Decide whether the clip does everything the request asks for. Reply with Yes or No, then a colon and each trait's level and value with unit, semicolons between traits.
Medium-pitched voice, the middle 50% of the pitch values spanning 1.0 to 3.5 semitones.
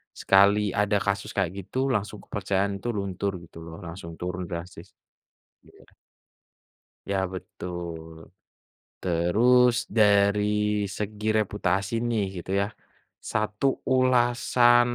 No: low, 100 Hz; average, 2.9 semitones